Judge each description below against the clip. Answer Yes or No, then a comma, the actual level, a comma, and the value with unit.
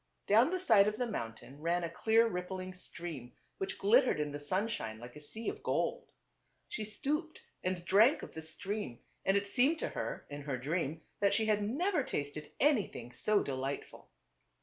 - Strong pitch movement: Yes, wide, 7.2 semitones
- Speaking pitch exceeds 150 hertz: Yes, medium, 185 Hz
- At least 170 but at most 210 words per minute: Yes, average, 185 wpm